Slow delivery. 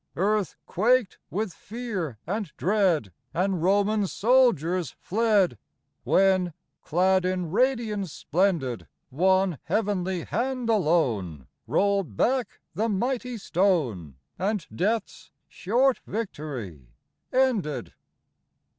Yes: slow, 95 wpm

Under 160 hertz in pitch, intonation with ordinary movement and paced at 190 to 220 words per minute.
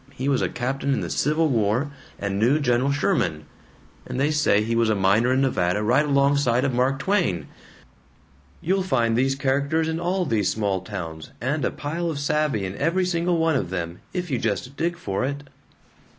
No: low, 135 Hz; wide, 6.0 semitones; average, 195 wpm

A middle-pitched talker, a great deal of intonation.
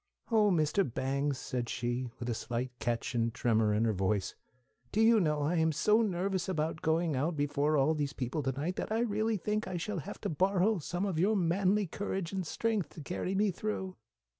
Yes: medium, 165 Hz; wide, 6.5 semitones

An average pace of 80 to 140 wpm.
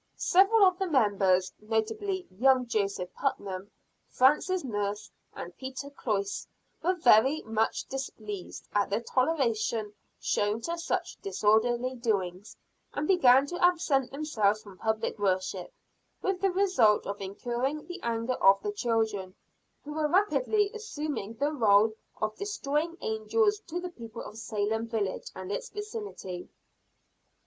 Yes: slow, 135 wpm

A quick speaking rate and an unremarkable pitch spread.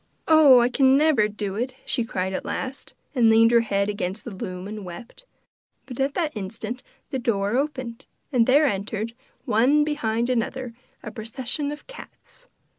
No: average, 170 wpm; average, 4.2 semitones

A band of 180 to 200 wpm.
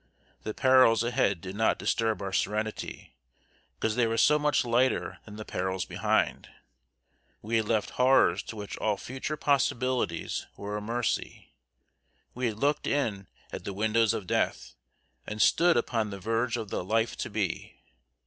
No: average, 160 wpm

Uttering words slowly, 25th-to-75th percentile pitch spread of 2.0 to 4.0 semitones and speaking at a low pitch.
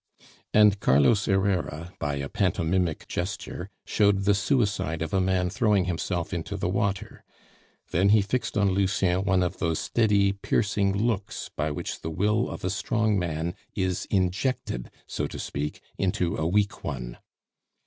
No: average, 155 wpm; average, 2.9 semitones; very low, 95 Hz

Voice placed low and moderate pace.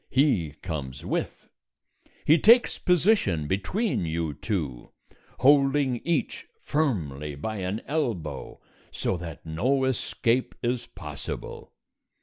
No: low, 110 Hz; slow, 105 wpm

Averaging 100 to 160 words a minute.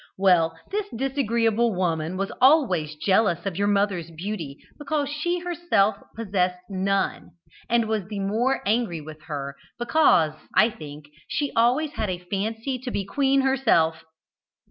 Yes: average, 145 wpm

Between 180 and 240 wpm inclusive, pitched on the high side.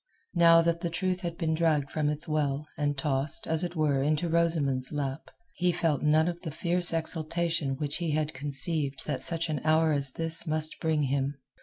No: average, 190 wpm; medium, 155 Hz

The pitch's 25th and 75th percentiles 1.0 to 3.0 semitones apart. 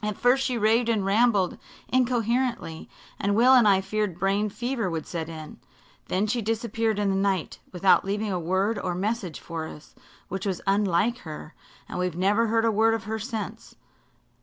No: average, 3.4 semitones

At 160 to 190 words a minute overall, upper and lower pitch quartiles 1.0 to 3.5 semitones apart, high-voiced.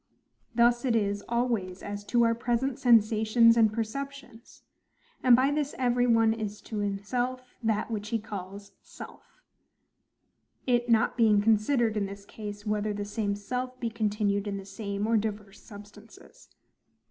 No: average, 145 wpm; narrow, 2.6 semitones; high, 220 Hz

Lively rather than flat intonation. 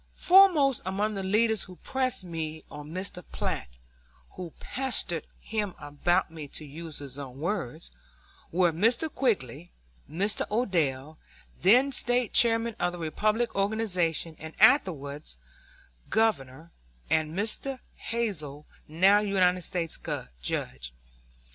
Yes: wide, 6.0 semitones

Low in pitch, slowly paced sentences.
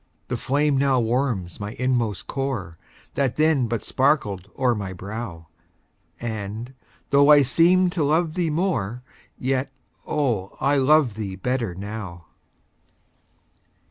Yes: low, 125 Hz; slow, 125 wpm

